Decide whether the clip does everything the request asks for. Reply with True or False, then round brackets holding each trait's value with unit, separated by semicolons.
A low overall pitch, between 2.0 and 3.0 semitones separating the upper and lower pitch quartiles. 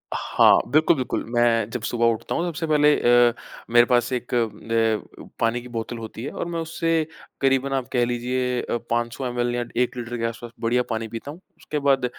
True (120 Hz; 2.4 semitones)